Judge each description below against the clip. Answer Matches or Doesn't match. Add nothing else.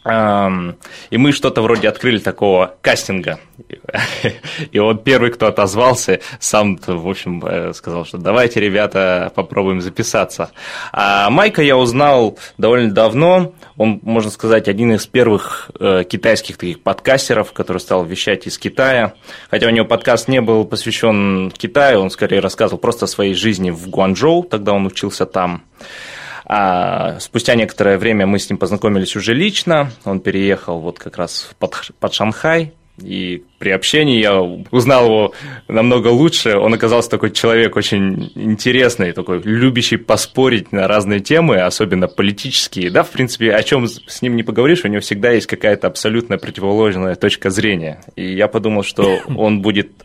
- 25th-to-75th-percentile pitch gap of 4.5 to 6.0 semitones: Doesn't match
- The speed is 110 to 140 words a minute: Doesn't match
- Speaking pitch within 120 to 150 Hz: Doesn't match